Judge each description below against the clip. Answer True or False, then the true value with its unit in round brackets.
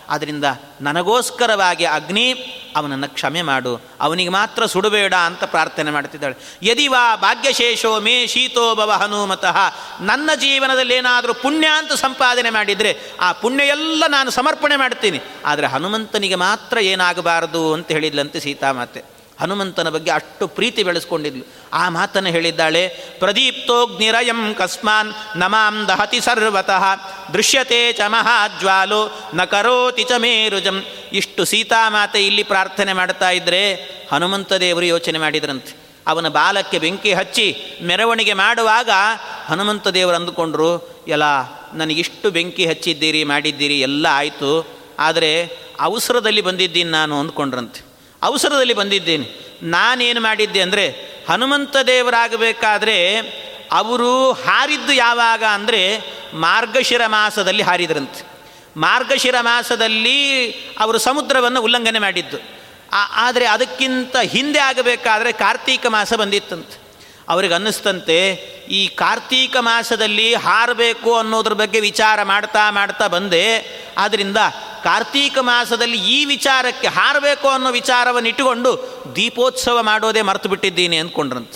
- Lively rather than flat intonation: True (5.7 semitones)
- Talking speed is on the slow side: False (100 wpm)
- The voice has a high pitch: True (210 Hz)